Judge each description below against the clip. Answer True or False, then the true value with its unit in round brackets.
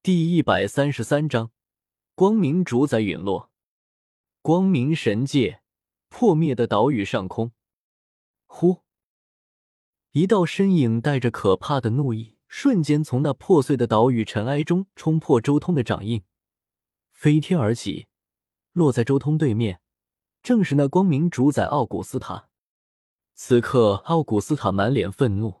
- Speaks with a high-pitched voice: False (135 Hz)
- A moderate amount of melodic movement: False (6.3 semitones)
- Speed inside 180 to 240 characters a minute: True (200 characters per minute)